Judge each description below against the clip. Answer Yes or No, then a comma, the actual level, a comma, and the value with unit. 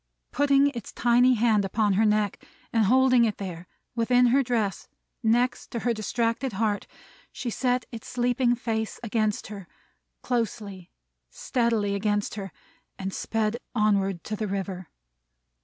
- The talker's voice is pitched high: Yes, high, 220 Hz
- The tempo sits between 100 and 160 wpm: Yes, average, 140 wpm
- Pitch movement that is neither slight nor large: Yes, average, 3.0 semitones